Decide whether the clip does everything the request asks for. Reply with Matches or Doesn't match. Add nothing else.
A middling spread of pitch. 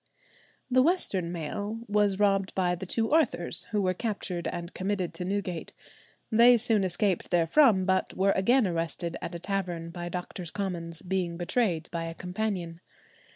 Matches